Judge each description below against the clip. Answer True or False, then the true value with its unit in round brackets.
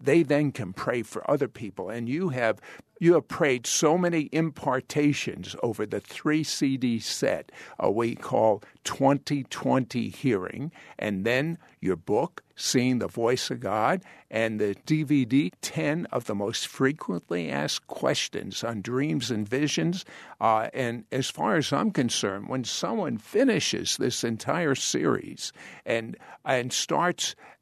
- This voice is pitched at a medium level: False (130 Hz)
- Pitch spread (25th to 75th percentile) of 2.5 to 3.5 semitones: False (4.4 semitones)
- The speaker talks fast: False (145 wpm)